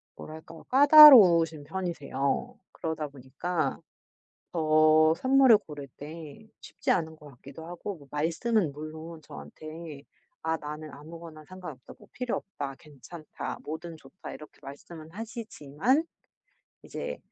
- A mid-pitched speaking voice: Yes, medium, 160 Hz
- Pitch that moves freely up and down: No, average, 3.3 semitones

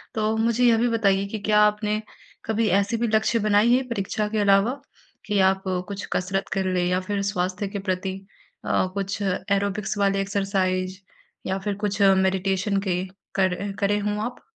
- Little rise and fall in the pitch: Yes, narrow, 1.9 semitones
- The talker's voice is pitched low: No, high, 200 Hz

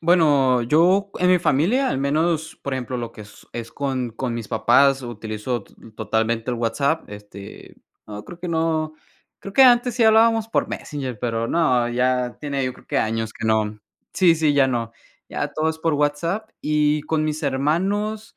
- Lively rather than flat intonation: Yes, wide, 5.8 semitones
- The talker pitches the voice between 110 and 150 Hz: Yes, medium, 140 Hz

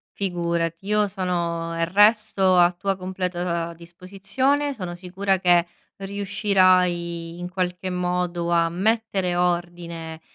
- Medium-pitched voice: Yes, medium, 180 Hz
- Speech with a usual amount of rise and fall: No, narrow, 2.2 semitones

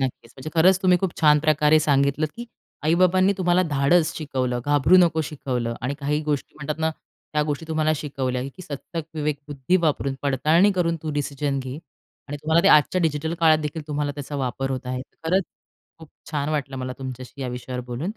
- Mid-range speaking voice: Yes, medium, 150 Hz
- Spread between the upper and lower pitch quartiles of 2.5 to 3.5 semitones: Yes, average, 3.0 semitones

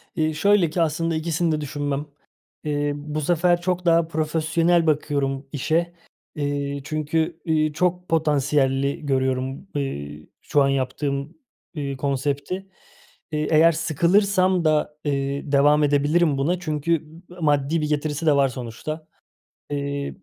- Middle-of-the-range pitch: Yes, medium, 150 Hz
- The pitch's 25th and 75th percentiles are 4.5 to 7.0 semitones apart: No, average, 2.7 semitones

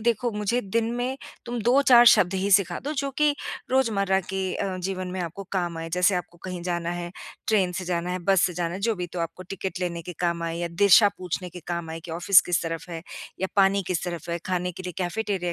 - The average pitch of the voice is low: No, medium, 185 Hz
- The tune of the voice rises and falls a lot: No, narrow, 2.4 semitones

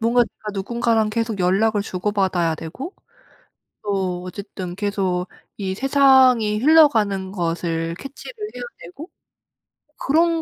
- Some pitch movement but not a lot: Yes, average, 4.9 semitones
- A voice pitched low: No, high, 210 Hz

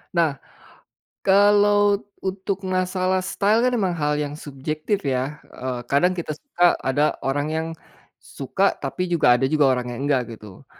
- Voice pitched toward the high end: No, medium, 160 Hz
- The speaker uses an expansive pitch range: Yes, wide, 5.7 semitones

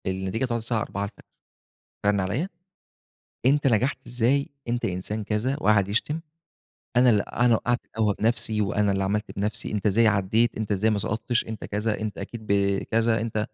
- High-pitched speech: No, low, 110 Hz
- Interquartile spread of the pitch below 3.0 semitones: Yes, narrow, 2.6 semitones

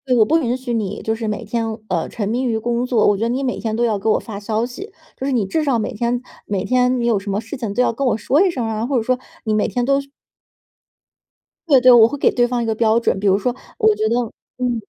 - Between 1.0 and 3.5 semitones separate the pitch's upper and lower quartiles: Yes, narrow, 2.6 semitones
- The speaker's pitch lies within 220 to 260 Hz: Yes, high, 235 Hz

